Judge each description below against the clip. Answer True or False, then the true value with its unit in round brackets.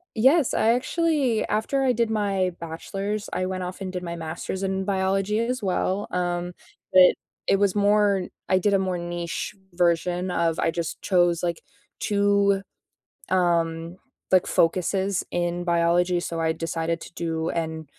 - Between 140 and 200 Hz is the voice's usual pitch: True (185 Hz)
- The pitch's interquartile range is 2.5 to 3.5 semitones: True (2.9 semitones)